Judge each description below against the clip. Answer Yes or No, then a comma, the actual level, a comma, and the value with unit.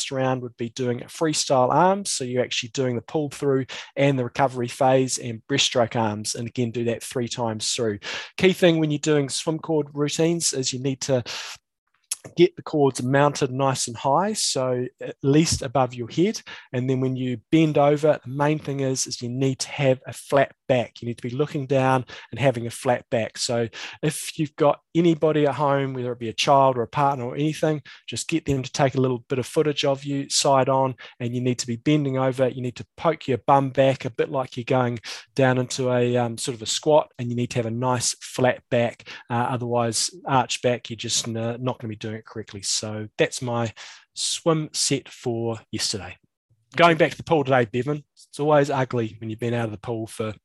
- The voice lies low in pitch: Yes, low, 130 Hz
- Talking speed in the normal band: No, fast, 220 wpm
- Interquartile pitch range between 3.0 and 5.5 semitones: Yes, average, 3.3 semitones